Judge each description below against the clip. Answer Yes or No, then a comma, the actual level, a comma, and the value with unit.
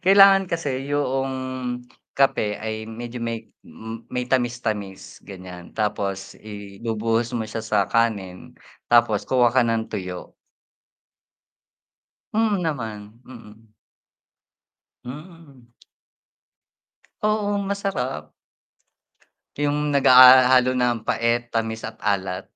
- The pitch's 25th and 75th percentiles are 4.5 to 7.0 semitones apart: No, average, 3.7 semitones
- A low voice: Yes, low, 120 Hz